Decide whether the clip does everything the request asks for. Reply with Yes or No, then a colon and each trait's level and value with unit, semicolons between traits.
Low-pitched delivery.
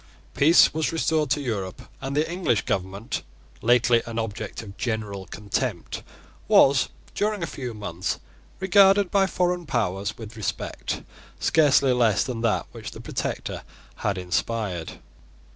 Yes: low, 120 Hz